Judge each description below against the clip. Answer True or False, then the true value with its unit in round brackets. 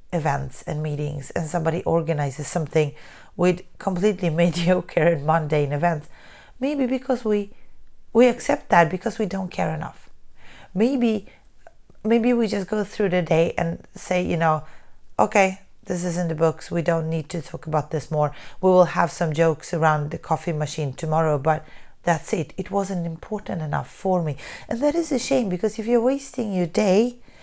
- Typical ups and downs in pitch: True (4.7 semitones)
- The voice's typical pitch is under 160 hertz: False (175 Hz)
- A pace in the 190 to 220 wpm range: False (175 wpm)